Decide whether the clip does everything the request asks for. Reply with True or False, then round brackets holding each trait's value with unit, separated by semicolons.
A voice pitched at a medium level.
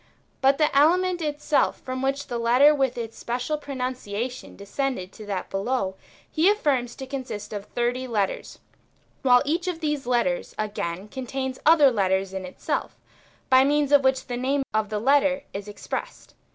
False (255 Hz)